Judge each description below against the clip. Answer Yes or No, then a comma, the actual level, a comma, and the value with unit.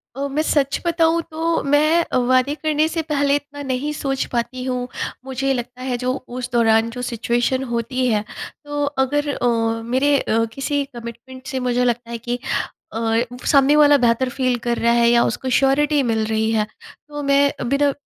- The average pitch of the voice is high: Yes, very high, 260 Hz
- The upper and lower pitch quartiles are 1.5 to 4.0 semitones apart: Yes, average, 3.3 semitones